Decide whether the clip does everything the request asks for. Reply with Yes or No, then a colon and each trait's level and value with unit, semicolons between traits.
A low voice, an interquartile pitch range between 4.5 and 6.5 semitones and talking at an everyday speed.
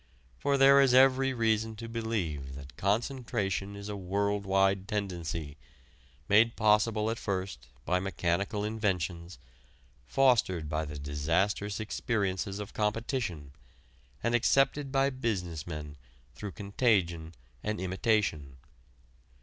No: low, 100 Hz; average, 4.8 semitones; slow, 115 wpm